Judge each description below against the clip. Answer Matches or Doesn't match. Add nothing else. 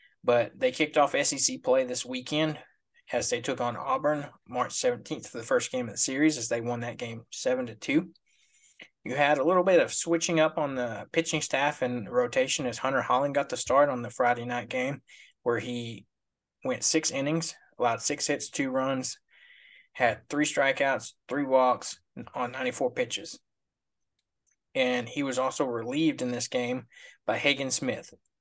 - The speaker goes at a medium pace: Matches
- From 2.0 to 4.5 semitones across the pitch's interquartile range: Doesn't match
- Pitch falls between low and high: Matches